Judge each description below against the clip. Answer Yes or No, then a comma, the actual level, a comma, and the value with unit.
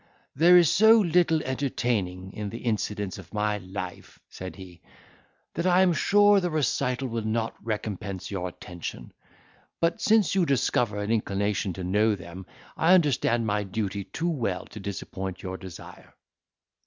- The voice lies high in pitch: No, low, 110 Hz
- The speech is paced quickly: No, average, 155 wpm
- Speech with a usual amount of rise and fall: No, wide, 8.4 semitones